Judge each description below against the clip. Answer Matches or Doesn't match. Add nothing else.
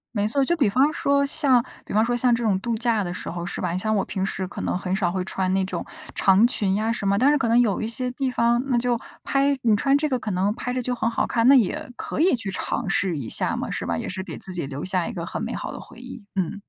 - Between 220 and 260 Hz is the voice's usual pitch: Matches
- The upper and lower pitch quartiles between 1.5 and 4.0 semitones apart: Doesn't match